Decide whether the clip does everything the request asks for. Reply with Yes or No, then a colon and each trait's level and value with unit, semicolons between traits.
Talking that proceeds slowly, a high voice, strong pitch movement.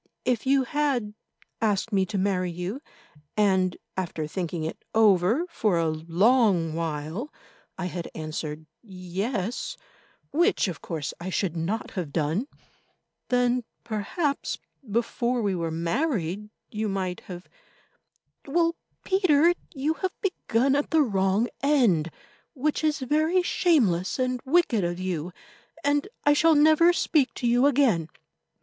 Yes: slow, 130 wpm; high, 215 Hz; wide, 8.0 semitones